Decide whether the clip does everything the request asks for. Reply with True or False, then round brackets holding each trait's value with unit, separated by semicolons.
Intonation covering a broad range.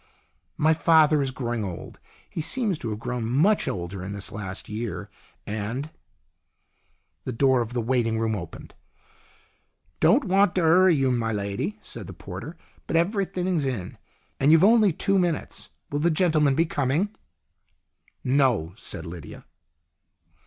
True (7.1 semitones)